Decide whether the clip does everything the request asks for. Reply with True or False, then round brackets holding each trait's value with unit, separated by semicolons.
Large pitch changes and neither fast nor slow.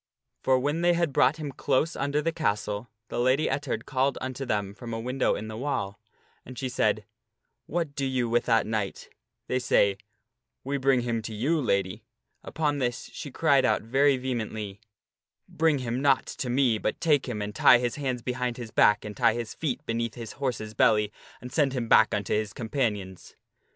False (4.0 semitones; 195 wpm)